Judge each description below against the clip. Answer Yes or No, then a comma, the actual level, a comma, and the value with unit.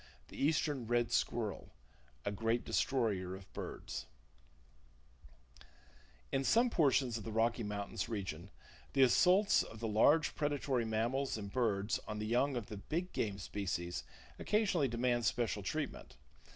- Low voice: Yes, low, 115 Hz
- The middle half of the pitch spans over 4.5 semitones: Yes, average, 4.9 semitones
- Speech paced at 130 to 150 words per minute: Yes, average, 140 wpm